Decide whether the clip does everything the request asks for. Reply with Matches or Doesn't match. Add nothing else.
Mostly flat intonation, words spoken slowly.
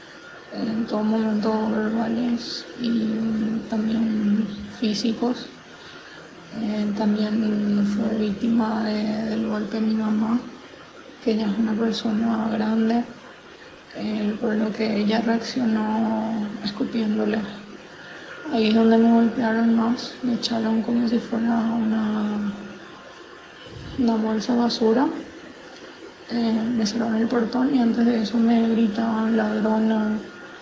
Matches